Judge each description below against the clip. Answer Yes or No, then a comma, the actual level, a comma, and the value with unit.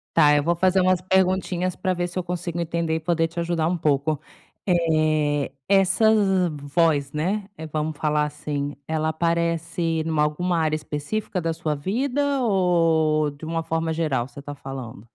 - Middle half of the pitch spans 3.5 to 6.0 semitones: No, average, 2.8 semitones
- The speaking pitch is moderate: Yes, medium, 165 Hz